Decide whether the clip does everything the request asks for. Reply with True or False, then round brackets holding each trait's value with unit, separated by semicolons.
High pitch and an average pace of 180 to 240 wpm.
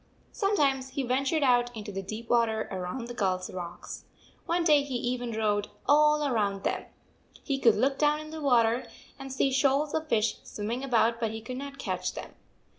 True (245 Hz; 190 wpm)